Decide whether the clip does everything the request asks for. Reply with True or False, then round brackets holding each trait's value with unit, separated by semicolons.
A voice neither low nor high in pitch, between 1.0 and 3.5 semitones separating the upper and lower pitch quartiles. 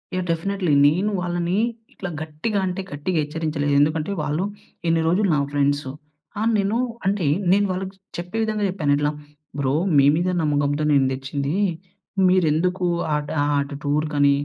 False (160 Hz; 4.2 semitones)